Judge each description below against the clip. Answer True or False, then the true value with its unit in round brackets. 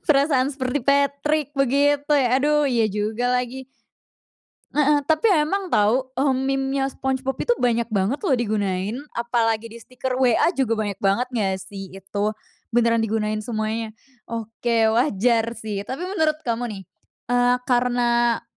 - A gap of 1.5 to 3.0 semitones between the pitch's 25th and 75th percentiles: False (3.6 semitones)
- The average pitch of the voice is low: False (245 Hz)